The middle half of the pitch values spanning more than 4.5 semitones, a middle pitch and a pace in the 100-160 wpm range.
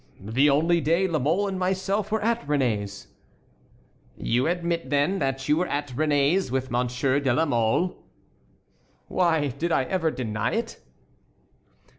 Yes: average, 5.2 semitones; medium, 150 Hz; average, 145 wpm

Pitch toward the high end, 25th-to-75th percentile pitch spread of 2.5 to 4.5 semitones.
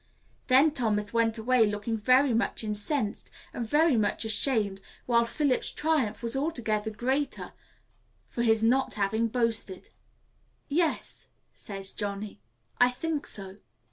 Yes: high, 230 Hz; average, 3.9 semitones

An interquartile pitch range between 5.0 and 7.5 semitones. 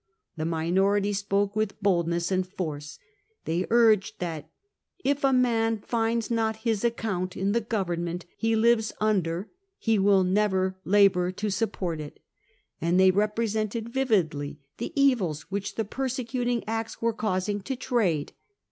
No: average, 3.7 semitones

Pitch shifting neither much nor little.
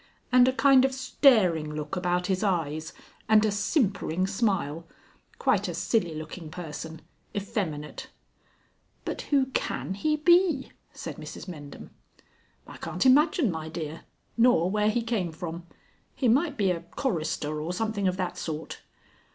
No: wide, 7.1 semitones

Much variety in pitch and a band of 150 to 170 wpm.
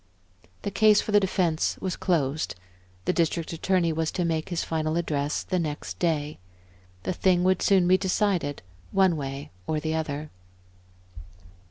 No: average, 3.3 semitones; average, 155 wpm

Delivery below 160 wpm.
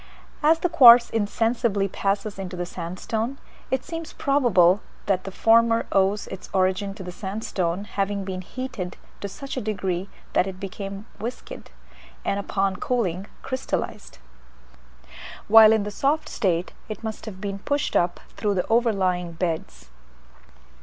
Yes: average, 145 wpm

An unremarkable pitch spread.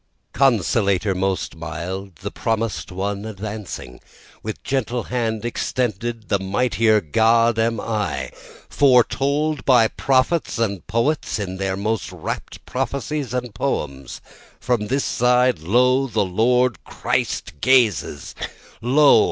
Yes: average, 4.4 semitones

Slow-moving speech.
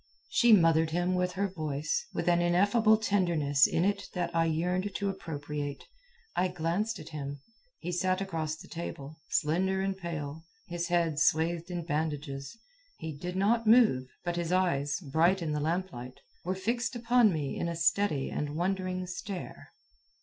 No: average, 165 wpm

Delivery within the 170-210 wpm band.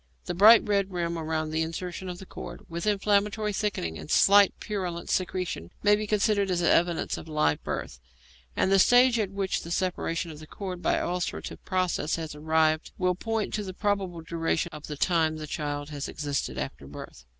Yes: average, 185 wpm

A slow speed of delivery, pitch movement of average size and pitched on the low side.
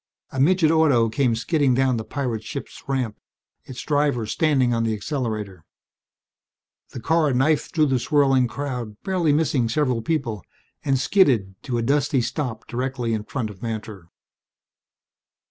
No: average, 145 wpm; average, 4.2 semitones; low, 130 Hz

